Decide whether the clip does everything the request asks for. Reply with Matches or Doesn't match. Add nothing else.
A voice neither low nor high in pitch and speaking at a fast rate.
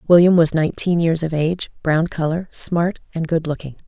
Doesn't match